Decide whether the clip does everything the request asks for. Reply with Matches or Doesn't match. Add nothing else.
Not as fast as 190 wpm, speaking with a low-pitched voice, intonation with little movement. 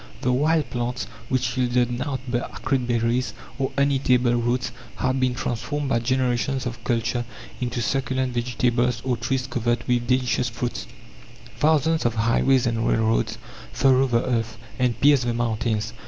Matches